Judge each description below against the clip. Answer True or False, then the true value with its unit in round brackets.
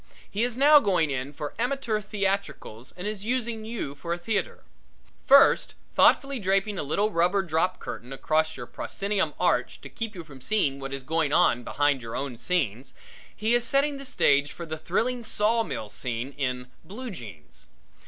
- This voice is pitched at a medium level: True (180 Hz)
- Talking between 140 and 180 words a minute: True (175 wpm)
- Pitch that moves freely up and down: True (7.9 semitones)